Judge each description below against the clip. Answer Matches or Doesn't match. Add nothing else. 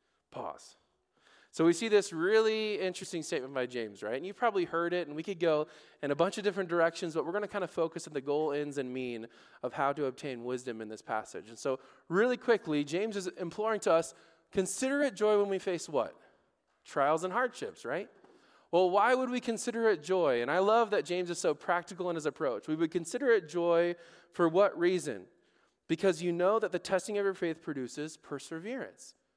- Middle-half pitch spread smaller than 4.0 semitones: Doesn't match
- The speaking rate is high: Matches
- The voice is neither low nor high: Matches